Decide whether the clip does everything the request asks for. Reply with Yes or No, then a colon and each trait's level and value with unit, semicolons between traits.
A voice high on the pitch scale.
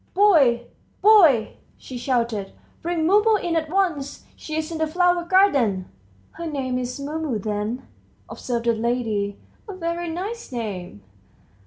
Yes: very high, 285 Hz